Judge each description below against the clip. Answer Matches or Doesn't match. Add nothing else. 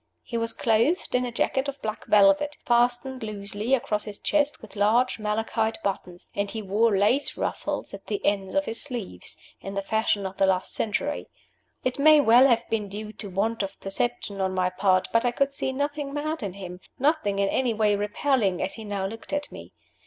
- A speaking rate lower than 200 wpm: Doesn't match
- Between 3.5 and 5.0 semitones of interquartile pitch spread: Matches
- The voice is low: Doesn't match